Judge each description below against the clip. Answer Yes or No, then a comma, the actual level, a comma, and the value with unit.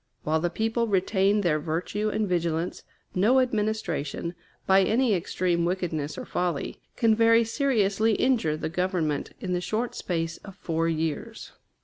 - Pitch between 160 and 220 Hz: Yes, medium, 185 Hz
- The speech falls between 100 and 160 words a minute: Yes, average, 145 wpm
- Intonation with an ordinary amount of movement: Yes, average, 4.7 semitones